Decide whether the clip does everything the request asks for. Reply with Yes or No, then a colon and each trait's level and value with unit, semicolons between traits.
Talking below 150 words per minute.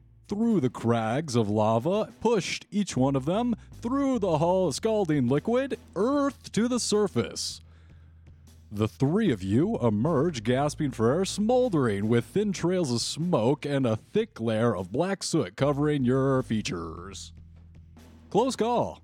Yes: average, 140 wpm